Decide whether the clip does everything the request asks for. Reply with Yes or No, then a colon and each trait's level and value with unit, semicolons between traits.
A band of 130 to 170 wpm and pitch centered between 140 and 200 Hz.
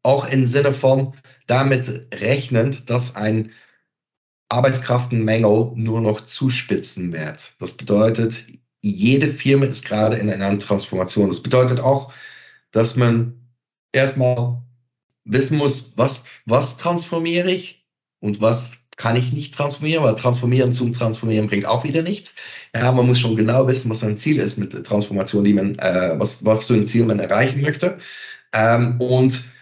No: average, 150 wpm; low, 125 Hz